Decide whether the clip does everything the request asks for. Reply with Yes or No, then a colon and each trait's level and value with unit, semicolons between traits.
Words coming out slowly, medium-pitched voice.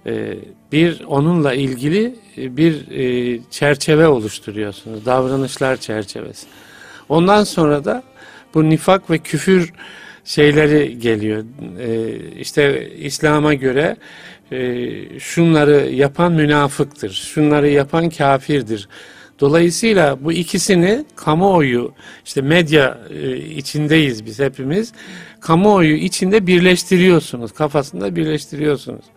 Yes: slow, 80 wpm; medium, 150 Hz